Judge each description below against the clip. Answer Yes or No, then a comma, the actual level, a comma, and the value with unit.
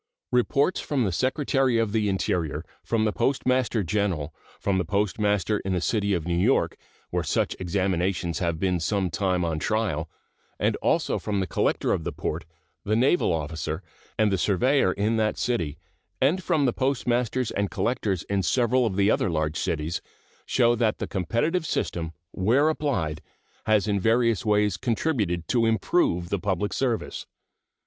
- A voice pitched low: Yes, low, 105 Hz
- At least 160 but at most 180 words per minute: Yes, average, 165 wpm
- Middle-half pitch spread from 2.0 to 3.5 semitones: No, average, 5.2 semitones